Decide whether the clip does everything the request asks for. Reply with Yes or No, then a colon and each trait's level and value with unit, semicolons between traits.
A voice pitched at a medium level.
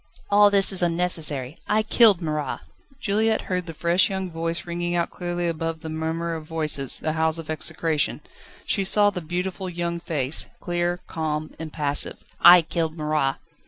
Yes: medium, 170 Hz